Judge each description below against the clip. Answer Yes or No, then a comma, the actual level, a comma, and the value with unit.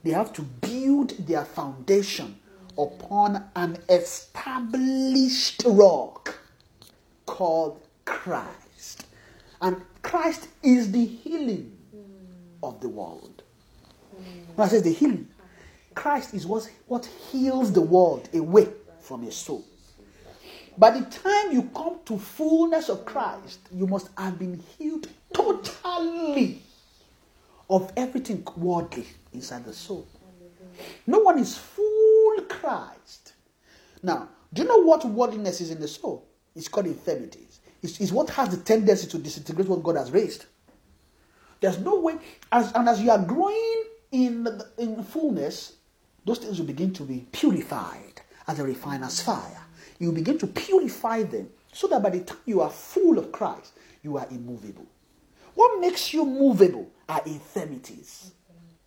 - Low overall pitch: No, high, 220 Hz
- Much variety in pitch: Yes, wide, 8.7 semitones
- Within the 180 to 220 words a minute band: No, slow, 135 wpm